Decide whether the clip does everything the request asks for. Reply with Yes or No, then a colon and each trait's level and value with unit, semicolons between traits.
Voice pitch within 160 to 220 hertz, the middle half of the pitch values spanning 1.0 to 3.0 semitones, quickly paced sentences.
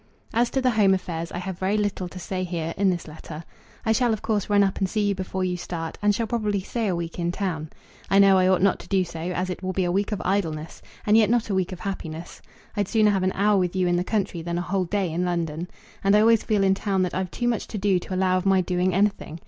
Yes: high, 190 Hz; narrow, 2.5 semitones; fast, 285 wpm